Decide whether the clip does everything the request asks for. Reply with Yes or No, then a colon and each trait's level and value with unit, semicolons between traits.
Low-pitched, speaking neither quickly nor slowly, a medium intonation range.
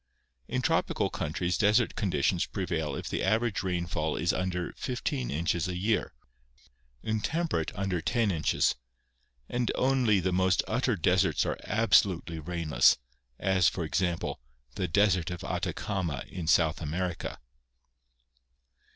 No: very low, 90 Hz; slow, 125 wpm; average, 4.0 semitones